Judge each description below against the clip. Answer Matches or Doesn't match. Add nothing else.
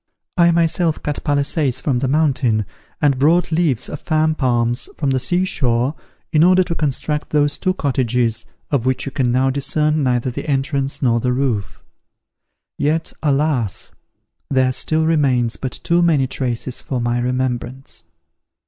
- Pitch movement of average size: Matches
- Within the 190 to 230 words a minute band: Doesn't match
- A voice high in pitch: Doesn't match